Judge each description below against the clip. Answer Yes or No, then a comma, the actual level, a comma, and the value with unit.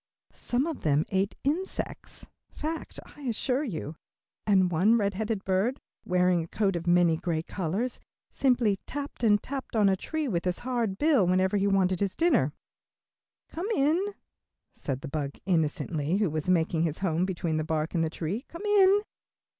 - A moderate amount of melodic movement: No, wide, 7.0 semitones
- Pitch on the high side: Yes, high, 195 Hz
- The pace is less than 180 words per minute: Yes, average, 170 wpm